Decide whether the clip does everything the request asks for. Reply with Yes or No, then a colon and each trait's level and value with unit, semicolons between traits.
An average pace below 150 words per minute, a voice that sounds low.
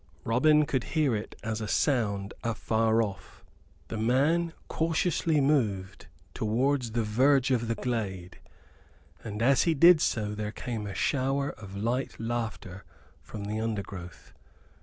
Yes: average, 140 wpm; low, 115 Hz